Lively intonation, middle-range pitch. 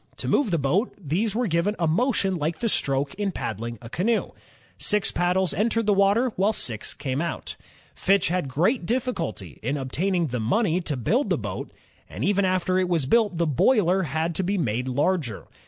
Yes: wide, 6.1 semitones; medium, 180 Hz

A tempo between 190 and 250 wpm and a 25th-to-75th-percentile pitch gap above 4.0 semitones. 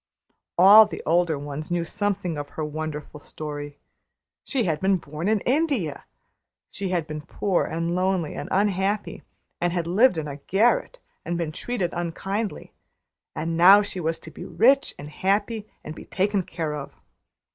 No: average, 165 wpm; average, 4.5 semitones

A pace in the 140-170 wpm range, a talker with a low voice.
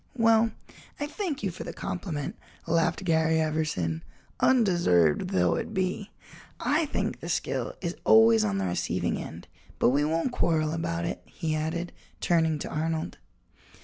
No: average, 150 wpm; medium, 165 Hz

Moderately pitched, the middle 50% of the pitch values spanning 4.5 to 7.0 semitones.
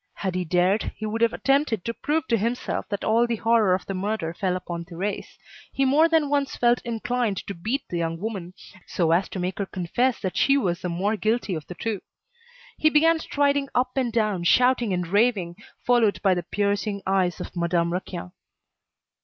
No: high, 210 Hz; average, 5.2 semitones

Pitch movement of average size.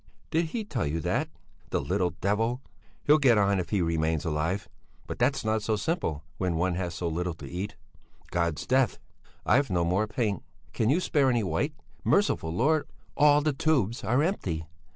No: wide, 8.0 semitones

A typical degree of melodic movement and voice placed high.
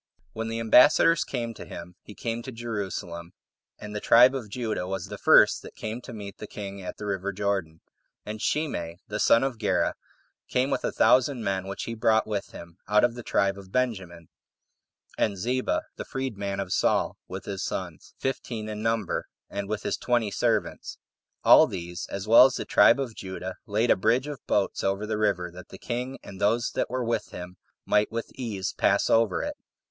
No: average, 3.4 semitones; low, 105 Hz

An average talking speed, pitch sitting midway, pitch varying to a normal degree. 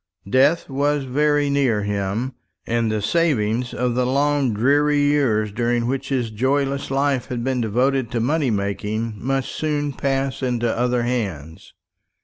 No: average, 145 wpm; low, 125 Hz; average, 3.5 semitones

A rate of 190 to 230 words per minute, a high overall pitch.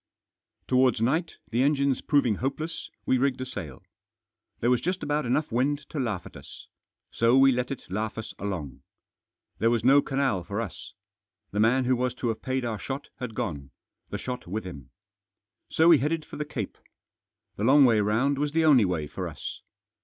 No: average, 195 wpm; low, 125 Hz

